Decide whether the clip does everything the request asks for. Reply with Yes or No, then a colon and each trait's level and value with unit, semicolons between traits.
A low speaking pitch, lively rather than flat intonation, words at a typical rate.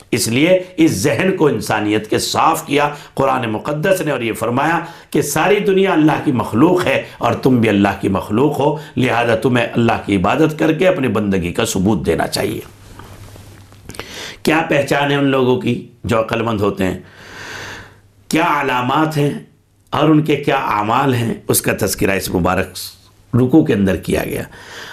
Yes: low, 115 Hz; wide, 6.3 semitones; average, 175 wpm